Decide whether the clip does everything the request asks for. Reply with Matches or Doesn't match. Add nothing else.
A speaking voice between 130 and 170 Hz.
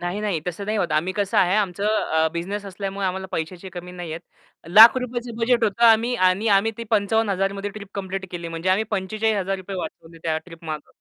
Doesn't match